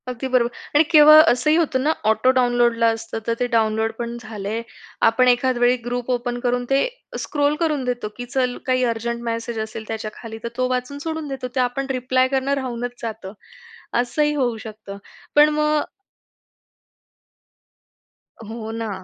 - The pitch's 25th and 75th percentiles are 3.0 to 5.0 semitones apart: No, narrow, 2.5 semitones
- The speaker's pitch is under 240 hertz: No, high, 245 Hz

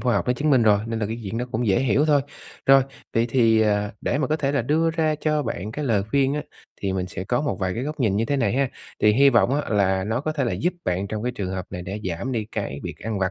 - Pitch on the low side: Yes, low, 115 Hz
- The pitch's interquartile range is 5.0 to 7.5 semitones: Yes, wide, 5.4 semitones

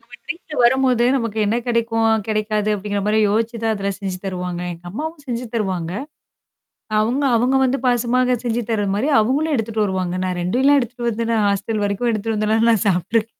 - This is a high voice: Yes, high, 225 Hz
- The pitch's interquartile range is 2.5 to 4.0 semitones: Yes, average, 3.0 semitones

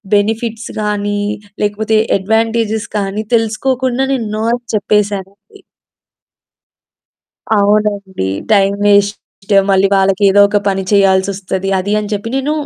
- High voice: Yes, high, 205 Hz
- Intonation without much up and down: Yes, narrow, 2.0 semitones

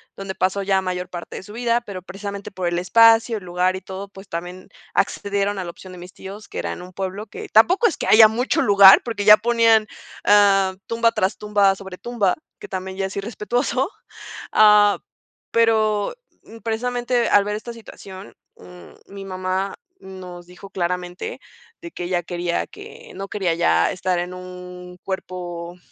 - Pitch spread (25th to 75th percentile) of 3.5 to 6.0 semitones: No, average, 2.9 semitones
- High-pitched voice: Yes, high, 195 Hz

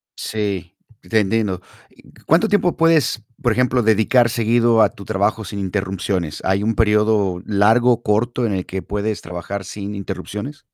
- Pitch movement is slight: No, average, 3.1 semitones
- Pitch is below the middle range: Yes, low, 105 Hz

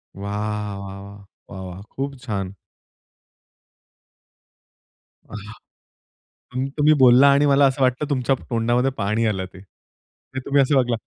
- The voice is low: Yes, low, 115 Hz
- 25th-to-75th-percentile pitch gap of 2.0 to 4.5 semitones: No, average, 5.0 semitones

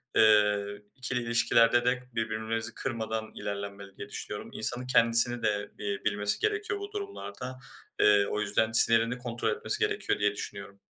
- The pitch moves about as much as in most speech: Yes, average, 3.0 semitones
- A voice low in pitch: Yes, low, 110 Hz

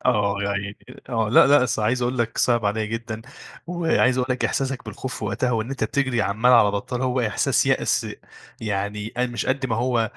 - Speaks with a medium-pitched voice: No, low, 120 Hz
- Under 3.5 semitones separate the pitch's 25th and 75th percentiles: Yes, average, 2.9 semitones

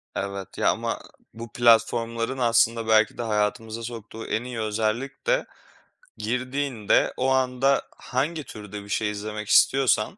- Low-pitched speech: Yes, low, 115 Hz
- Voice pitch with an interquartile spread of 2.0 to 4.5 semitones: Yes, average, 2.9 semitones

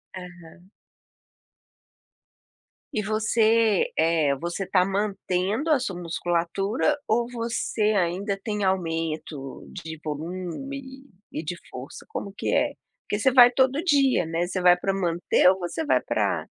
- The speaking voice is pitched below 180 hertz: No, high, 190 Hz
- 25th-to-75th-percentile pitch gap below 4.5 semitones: No, average, 4.8 semitones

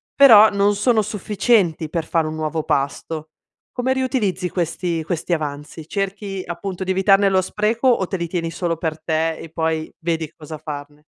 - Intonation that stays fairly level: No, average, 3.9 semitones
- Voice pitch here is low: No, medium, 175 Hz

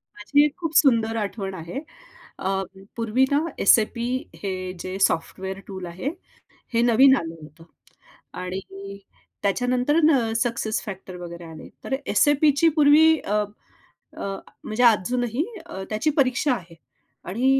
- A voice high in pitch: Yes, high, 225 Hz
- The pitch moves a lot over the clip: Yes, wide, 5.7 semitones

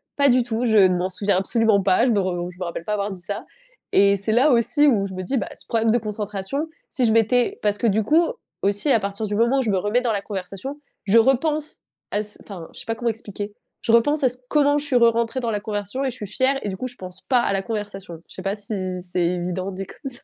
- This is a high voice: Yes, high, 215 Hz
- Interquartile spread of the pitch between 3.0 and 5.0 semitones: Yes, average, 4.0 semitones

